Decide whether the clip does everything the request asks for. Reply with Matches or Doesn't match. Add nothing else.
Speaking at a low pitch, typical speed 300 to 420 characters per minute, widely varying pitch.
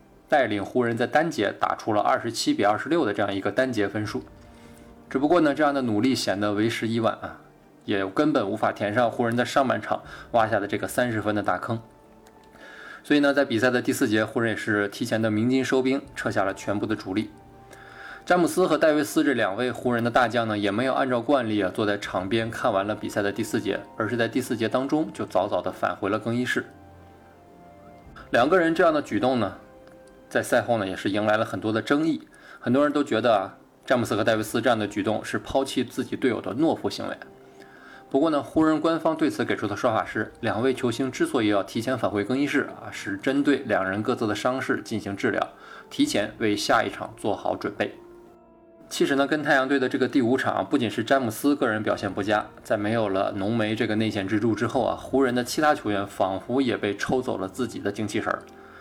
Doesn't match